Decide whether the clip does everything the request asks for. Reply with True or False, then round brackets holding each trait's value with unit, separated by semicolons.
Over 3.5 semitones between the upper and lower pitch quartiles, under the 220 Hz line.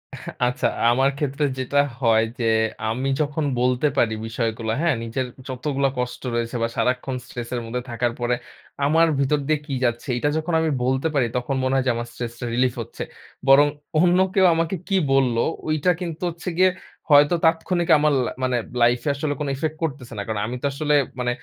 True (3.9 semitones; 135 Hz)